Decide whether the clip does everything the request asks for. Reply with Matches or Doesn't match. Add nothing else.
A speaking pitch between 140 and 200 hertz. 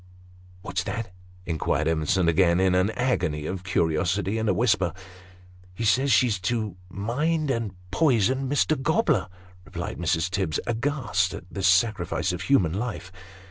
Doesn't match